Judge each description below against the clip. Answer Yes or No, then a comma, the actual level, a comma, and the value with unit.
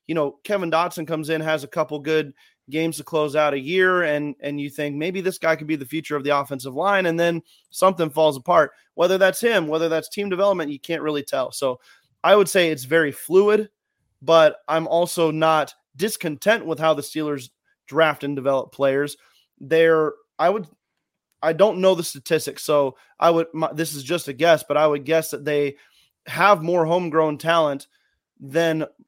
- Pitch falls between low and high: Yes, medium, 160 Hz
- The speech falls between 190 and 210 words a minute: Yes, average, 195 wpm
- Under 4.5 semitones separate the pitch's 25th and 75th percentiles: Yes, average, 2.7 semitones